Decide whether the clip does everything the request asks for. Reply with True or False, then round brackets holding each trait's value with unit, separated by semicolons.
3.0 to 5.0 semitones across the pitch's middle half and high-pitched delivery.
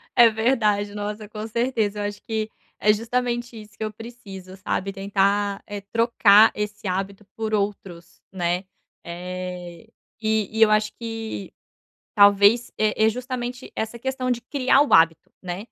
False (2.6 semitones; 210 Hz)